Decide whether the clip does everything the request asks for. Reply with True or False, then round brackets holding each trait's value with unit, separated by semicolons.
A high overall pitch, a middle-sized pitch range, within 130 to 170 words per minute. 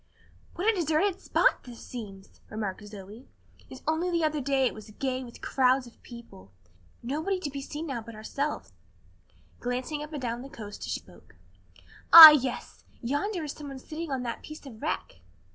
False (265 Hz; 4.7 semitones; 180 wpm)